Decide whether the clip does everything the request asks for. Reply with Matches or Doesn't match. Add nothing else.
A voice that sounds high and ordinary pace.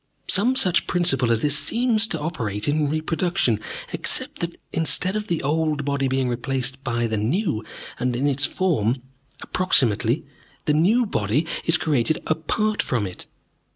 Doesn't match